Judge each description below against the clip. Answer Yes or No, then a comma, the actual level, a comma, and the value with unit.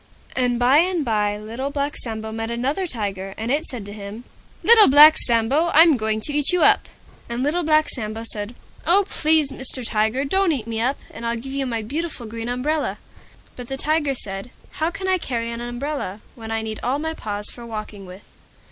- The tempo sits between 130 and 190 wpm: No, fast, 205 wpm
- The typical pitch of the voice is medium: No, high, 245 Hz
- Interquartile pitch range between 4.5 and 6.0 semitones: Yes, average, 5.1 semitones